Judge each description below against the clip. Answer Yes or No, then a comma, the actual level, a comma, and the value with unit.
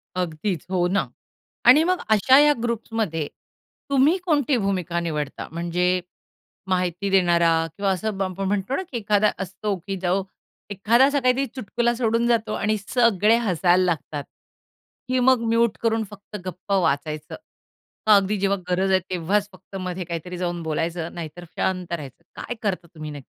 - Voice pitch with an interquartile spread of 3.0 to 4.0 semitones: No, average, 4.4 semitones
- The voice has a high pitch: Yes, high, 195 Hz